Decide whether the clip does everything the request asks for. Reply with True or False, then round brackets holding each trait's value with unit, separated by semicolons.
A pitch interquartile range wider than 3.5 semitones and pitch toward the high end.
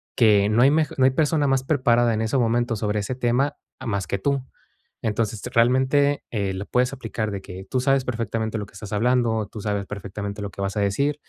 False (4.1 semitones; 115 Hz)